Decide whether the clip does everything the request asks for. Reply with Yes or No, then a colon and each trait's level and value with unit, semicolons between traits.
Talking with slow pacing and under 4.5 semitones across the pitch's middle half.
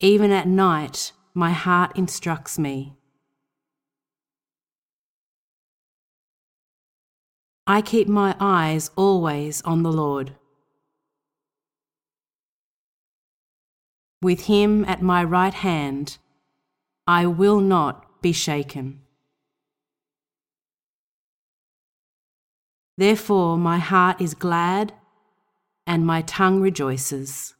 No: slow, 75 wpm; average, 5.0 semitones